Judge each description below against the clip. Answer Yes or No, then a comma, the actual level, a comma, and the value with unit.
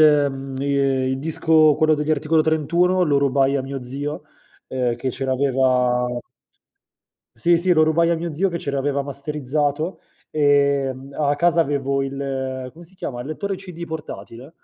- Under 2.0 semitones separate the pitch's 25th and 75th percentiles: No, average, 2.8 semitones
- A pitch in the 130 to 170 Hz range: Yes, medium, 140 Hz